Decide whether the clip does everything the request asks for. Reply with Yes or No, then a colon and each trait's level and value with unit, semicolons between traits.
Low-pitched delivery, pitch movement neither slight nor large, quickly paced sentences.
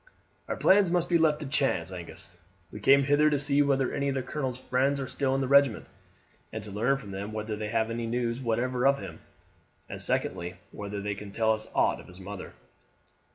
Yes: low, 125 Hz; average, 5.0 semitones; fast, 215 wpm